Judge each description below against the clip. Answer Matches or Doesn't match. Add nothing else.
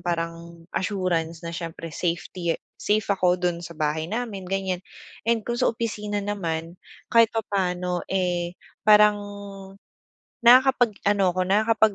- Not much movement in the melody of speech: Doesn't match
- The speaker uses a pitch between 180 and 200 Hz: Matches